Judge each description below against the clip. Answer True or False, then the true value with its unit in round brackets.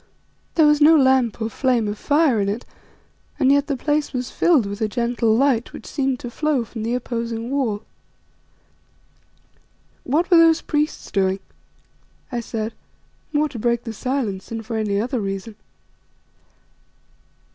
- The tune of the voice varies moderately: True (4.3 semitones)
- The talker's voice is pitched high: True (245 Hz)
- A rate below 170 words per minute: True (155 wpm)